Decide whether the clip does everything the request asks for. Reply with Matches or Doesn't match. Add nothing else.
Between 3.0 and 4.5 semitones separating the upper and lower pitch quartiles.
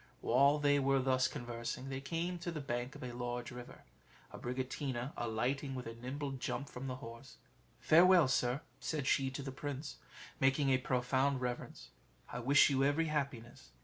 Doesn't match